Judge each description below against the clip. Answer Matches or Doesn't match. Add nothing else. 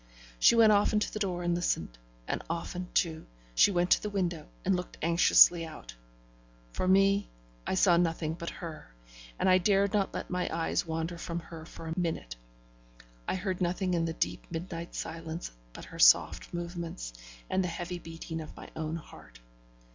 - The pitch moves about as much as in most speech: Doesn't match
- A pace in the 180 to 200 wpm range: Matches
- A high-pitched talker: Doesn't match